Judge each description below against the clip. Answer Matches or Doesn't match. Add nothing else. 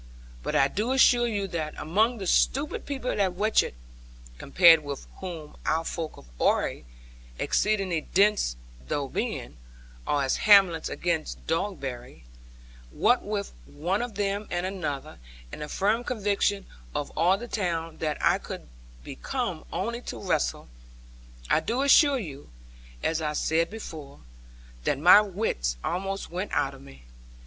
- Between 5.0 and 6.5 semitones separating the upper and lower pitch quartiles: Matches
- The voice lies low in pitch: Doesn't match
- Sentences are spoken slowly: Doesn't match